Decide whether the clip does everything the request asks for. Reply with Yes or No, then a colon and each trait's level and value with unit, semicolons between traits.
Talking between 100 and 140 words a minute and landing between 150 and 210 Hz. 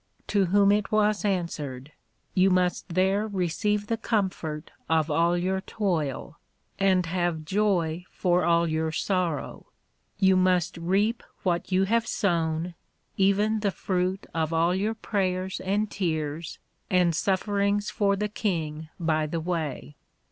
Yes: slow, 135 wpm; medium, 185 Hz